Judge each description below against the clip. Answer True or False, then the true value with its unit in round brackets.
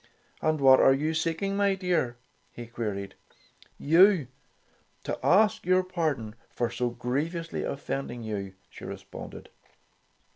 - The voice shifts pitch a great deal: True (6.7 semitones)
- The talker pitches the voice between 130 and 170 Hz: True (140 Hz)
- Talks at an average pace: False (125 wpm)